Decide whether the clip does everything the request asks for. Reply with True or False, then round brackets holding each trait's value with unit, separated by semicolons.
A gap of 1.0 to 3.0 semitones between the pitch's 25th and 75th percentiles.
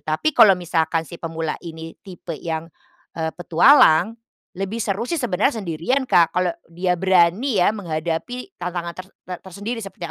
False (3.7 semitones)